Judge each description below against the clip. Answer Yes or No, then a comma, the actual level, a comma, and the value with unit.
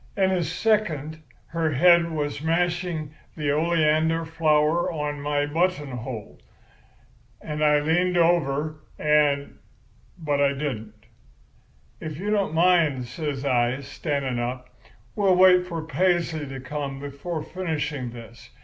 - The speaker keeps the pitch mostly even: No, average, 3.3 semitones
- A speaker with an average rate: No, slow, 120 wpm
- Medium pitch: Yes, medium, 150 Hz